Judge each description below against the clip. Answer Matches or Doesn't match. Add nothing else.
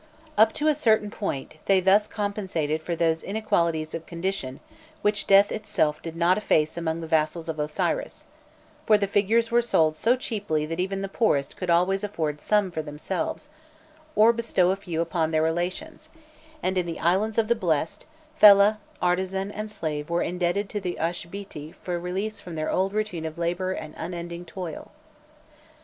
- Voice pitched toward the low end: Doesn't match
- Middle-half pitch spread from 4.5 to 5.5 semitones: Doesn't match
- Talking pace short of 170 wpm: Doesn't match